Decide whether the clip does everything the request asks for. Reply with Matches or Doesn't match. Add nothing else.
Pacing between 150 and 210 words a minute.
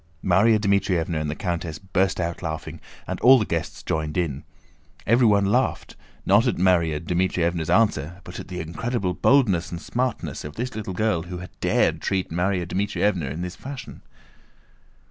Matches